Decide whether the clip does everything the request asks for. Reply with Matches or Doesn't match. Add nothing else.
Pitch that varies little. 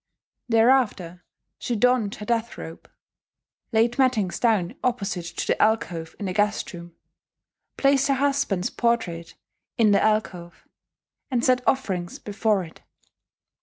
Doesn't match